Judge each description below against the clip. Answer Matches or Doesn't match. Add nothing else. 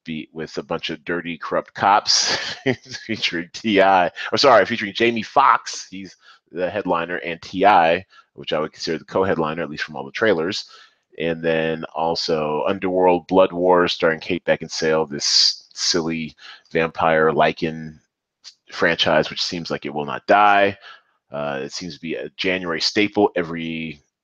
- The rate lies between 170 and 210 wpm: Doesn't match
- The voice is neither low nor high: Doesn't match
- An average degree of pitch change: Matches